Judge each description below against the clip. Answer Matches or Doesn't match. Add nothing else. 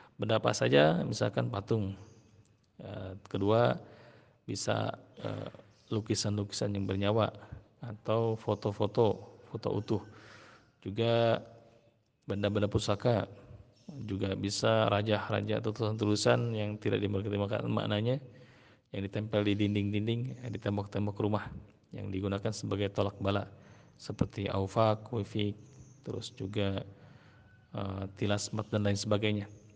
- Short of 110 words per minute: Matches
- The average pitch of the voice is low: Matches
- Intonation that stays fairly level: Matches